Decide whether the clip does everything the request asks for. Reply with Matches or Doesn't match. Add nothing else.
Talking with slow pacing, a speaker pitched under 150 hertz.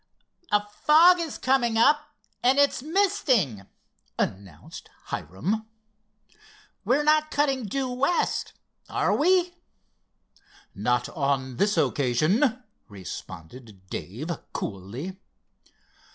Doesn't match